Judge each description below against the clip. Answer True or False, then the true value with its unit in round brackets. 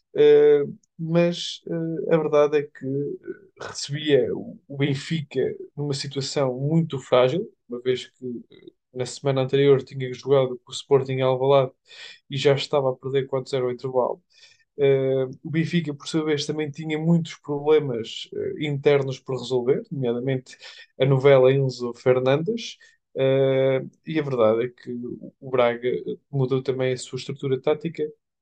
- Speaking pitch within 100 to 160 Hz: True (140 Hz)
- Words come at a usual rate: True (140 wpm)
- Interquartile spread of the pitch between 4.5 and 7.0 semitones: False (3.7 semitones)